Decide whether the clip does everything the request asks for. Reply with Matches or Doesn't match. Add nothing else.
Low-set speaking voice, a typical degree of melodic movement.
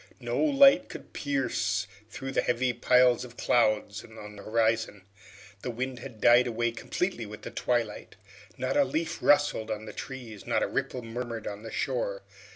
Matches